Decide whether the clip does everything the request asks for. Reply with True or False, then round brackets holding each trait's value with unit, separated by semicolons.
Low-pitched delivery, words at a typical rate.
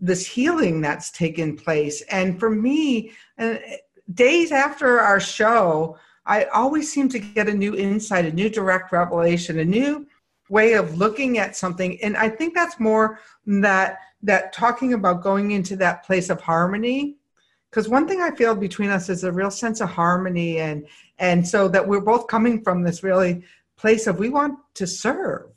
False (200 Hz; 175 wpm)